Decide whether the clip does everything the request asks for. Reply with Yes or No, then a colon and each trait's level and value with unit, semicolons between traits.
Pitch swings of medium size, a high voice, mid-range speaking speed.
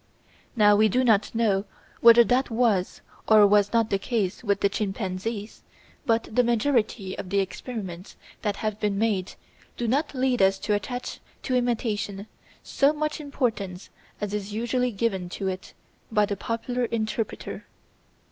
Yes: average, 3.1 semitones; high, 215 Hz; average, 155 wpm